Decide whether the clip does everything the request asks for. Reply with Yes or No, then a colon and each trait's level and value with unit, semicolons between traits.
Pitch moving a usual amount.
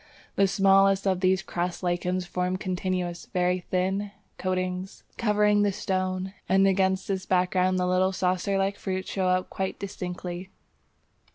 No: narrow, 1.0 semitones